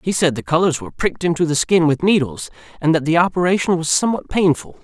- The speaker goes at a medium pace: No, fast, 225 wpm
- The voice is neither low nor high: Yes, medium, 165 Hz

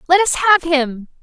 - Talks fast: No, average, 195 wpm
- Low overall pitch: No, very high, 315 Hz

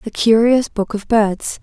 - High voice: Yes, high, 220 Hz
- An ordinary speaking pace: Yes, average, 185 wpm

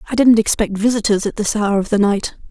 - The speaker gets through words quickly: Yes, fast, 240 wpm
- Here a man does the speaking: No, female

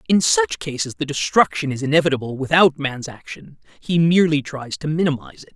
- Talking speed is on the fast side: No, average, 175 wpm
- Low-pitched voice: No, medium, 150 Hz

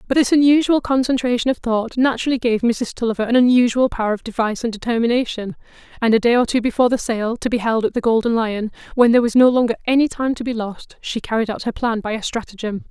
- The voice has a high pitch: Yes, high, 235 Hz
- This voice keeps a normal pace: No, fast, 230 wpm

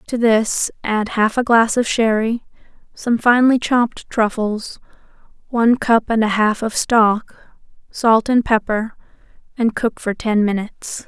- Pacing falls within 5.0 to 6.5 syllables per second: No, 4.3 syllables/s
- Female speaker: Yes, female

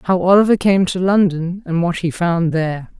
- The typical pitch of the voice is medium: Yes, medium, 175 Hz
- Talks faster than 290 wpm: No, average, 200 wpm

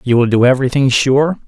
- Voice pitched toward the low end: Yes, low, 130 Hz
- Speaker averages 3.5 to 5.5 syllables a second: No, 6.1 syllables/s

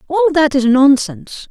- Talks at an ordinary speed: Yes, average, 160 wpm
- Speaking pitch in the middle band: No, very high, 300 Hz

